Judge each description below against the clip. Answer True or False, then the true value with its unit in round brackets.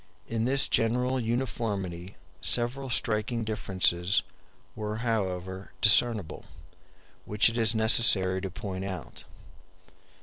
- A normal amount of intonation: True (3.7 semitones)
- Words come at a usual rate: False (100 wpm)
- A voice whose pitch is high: False (110 Hz)